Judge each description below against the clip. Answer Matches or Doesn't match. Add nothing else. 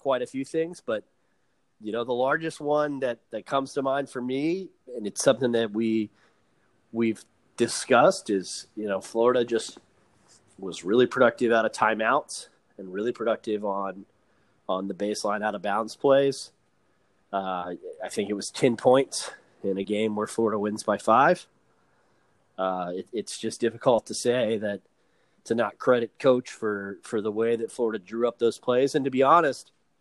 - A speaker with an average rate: Matches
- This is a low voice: Matches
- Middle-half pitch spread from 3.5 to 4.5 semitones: Matches